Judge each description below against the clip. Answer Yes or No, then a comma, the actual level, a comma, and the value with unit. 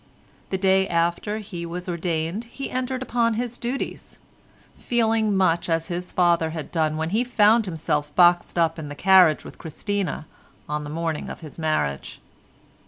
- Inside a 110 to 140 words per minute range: No, average, 160 wpm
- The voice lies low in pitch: No, medium, 175 Hz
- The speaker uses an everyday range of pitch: Yes, average, 4.8 semitones